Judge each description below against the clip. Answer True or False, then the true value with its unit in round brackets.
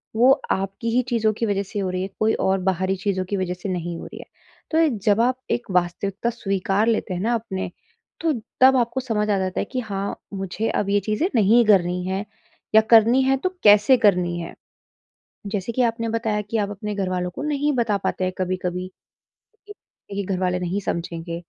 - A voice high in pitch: True (200 Hz)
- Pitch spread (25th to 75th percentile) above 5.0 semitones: False (3.7 semitones)